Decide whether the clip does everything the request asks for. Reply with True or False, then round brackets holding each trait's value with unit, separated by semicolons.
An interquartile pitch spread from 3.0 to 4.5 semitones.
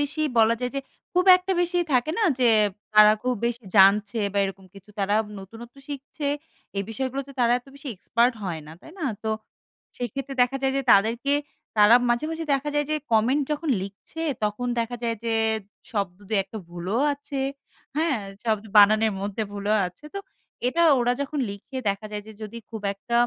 False (4.9 semitones)